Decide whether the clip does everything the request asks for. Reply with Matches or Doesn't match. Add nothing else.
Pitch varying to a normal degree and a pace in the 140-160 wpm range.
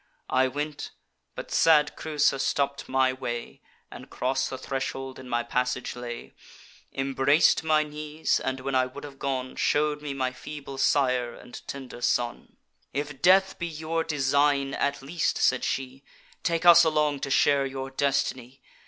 Doesn't match